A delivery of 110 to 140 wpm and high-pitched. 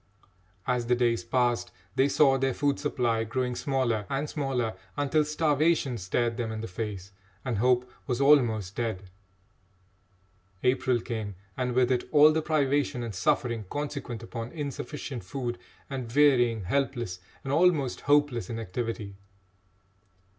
No: slow, 135 wpm; low, 125 Hz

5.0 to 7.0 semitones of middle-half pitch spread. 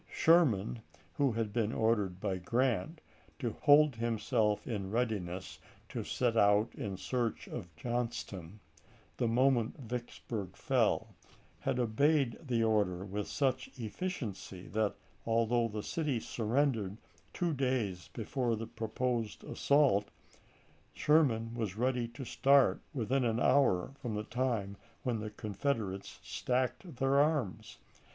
No: average, 3.7 semitones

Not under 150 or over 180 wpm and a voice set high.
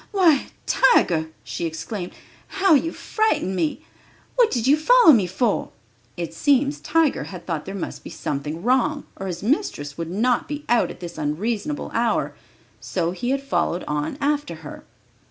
Yes: average, 165 wpm; high, 230 Hz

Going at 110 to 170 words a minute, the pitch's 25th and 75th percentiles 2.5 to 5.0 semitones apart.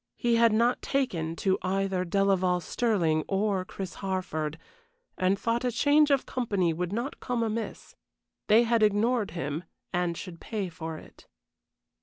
Yes: average, 150 wpm; average, 4.5 semitones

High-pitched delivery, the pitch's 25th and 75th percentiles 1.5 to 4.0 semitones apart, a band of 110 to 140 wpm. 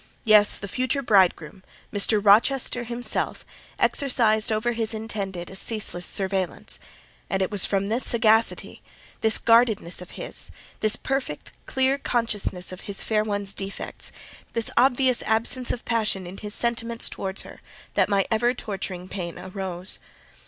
Yes: high, 215 Hz; average, 3.5 semitones; slow, 135 wpm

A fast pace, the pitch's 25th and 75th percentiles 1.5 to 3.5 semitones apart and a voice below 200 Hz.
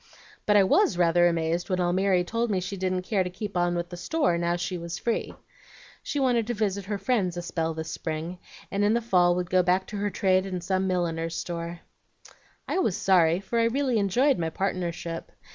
Yes: fast, 210 wpm; average, 2.9 semitones; medium, 185 Hz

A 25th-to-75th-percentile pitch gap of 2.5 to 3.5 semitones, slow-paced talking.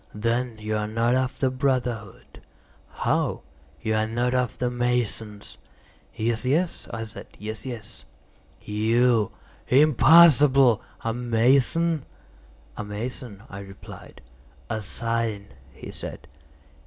Yes: average, 2.8 semitones; slow, 115 wpm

